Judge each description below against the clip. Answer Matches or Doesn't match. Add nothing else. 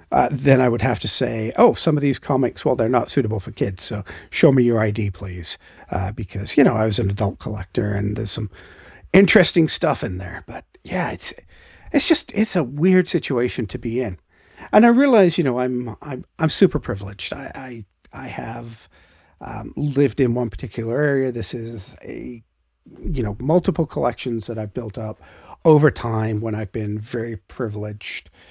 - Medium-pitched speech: Doesn't match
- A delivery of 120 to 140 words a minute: Doesn't match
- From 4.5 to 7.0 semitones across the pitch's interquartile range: Matches